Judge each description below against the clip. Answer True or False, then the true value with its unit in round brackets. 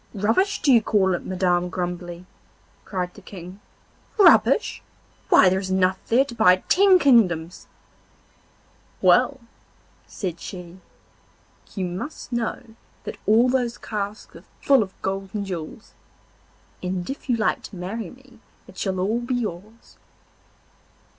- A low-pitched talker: False (200 Hz)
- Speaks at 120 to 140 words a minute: True (135 wpm)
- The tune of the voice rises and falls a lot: False (4.5 semitones)